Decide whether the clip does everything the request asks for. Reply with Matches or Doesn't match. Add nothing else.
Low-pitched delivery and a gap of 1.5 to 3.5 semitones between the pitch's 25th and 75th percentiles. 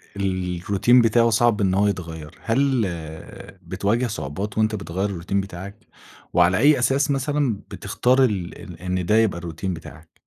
Doesn't match